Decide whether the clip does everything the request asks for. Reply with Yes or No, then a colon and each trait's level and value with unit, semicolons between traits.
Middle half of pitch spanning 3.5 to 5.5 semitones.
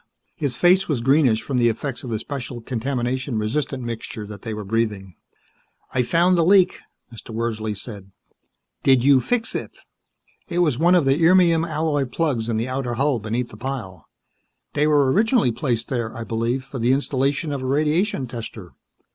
Yes: average, 4.5 semitones